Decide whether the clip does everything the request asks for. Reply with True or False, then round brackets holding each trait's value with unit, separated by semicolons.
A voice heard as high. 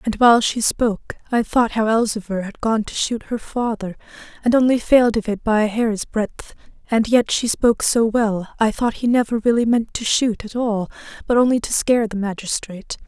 True (225 Hz)